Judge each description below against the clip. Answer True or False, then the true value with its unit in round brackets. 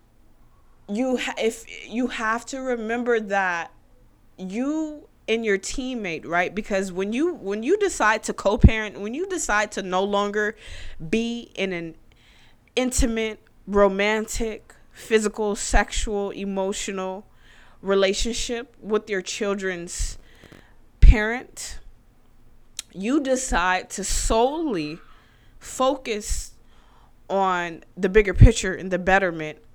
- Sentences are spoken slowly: True (105 wpm)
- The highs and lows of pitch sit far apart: False (3.8 semitones)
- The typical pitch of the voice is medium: False (205 Hz)